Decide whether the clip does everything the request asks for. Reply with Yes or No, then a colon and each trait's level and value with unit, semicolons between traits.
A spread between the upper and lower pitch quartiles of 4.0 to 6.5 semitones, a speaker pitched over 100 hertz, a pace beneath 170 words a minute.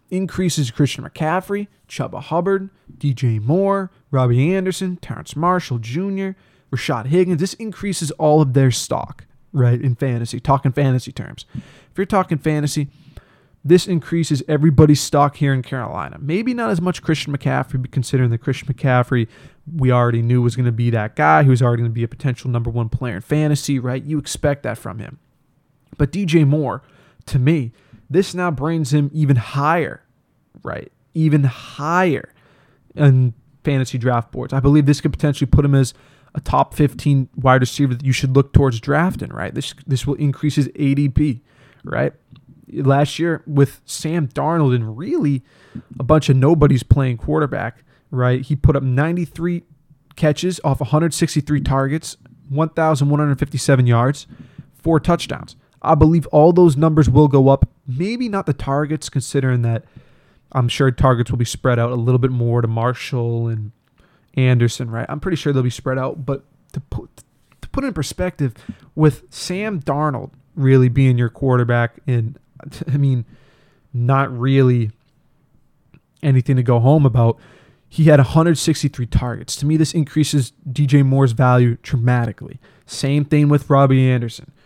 No: average, 3.2 semitones; medium, 140 Hz; average, 160 wpm